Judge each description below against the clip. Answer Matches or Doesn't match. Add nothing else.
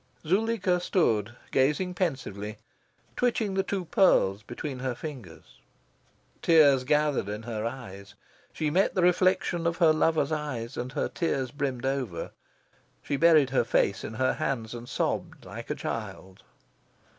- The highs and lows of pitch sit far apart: Matches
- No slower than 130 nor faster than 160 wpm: Matches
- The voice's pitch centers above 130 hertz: Matches